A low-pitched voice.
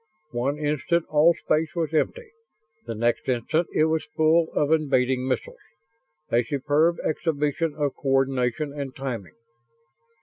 No: medium, 150 Hz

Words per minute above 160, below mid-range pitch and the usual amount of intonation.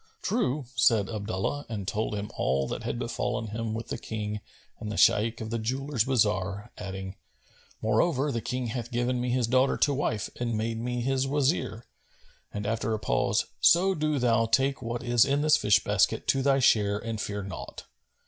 Yes: average, 185 wpm; low, 115 Hz; average, 3.8 semitones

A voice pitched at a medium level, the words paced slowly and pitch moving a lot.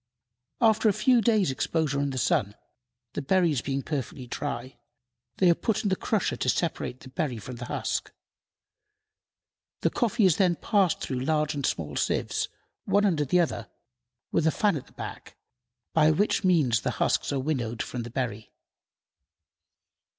No: medium, 150 Hz; average, 165 wpm; wide, 6.7 semitones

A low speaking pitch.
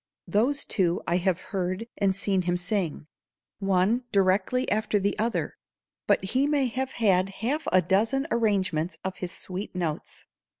No: high, 195 Hz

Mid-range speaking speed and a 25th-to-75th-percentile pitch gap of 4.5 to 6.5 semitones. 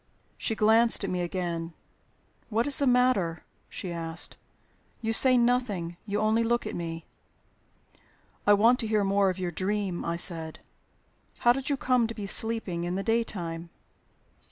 Yes: average, 160 wpm; average, 4.9 semitones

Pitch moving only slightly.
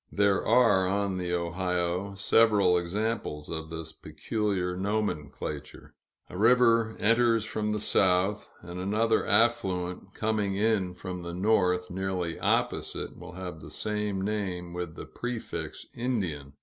No: average, 3.3 semitones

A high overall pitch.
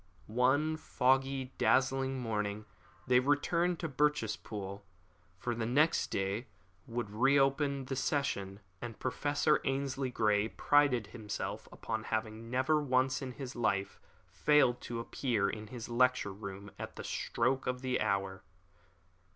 No: low, 125 Hz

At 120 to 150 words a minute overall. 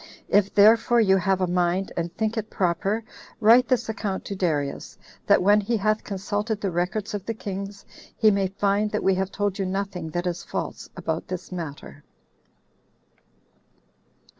No: average, 165 wpm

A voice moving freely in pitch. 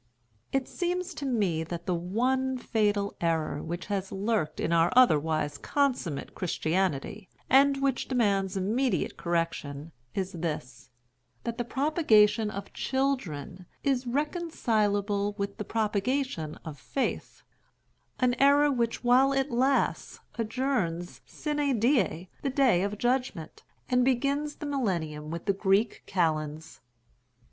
Yes: wide, 7.3 semitones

